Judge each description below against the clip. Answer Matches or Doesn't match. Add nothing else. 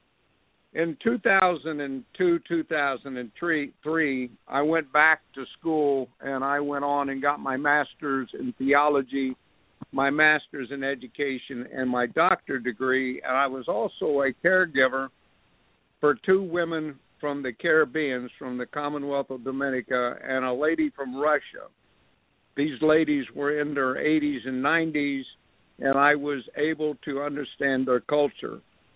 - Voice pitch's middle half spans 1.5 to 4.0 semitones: Matches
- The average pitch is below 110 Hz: Doesn't match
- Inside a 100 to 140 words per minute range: Matches